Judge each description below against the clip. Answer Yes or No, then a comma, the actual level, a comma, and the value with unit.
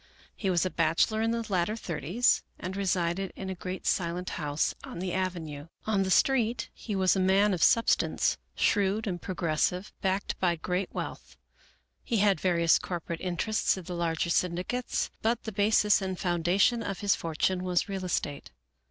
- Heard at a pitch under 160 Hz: No, medium, 185 Hz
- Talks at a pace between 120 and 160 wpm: No, average, 170 wpm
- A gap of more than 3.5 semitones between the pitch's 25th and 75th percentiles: No, average, 2.8 semitones